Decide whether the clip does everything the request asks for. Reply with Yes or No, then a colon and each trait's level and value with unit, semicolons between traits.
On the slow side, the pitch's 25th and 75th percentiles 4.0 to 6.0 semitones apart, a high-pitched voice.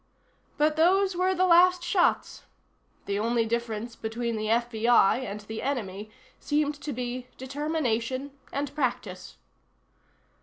Yes: slow, 120 wpm; average, 5.3 semitones; very high, 250 Hz